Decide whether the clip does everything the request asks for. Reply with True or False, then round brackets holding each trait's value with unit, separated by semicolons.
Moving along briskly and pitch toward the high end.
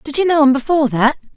True (265 wpm; 285 Hz)